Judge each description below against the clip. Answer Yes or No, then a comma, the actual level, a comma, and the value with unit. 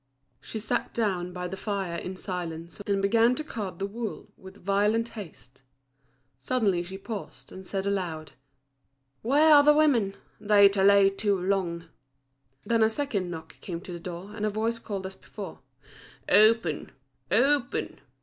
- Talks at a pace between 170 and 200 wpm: No, average, 155 wpm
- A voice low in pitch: No, high, 200 Hz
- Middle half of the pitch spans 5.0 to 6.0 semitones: No, average, 3.7 semitones